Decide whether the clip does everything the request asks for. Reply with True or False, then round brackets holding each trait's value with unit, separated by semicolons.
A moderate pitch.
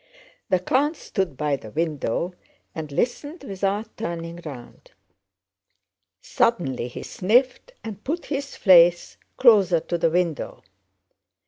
True (180 Hz)